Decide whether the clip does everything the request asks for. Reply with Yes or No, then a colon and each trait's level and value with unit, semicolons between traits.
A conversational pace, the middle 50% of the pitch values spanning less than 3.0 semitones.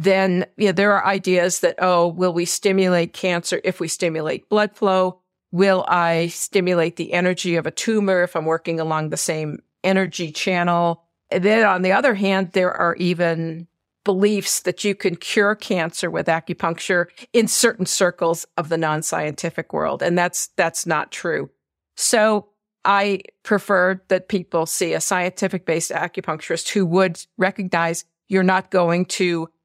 Yes: average, 160 wpm; narrow, 2.4 semitones